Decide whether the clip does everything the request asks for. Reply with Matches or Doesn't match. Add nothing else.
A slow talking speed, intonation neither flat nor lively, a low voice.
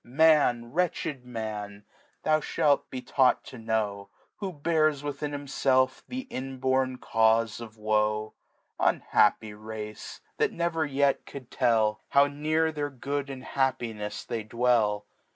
Matches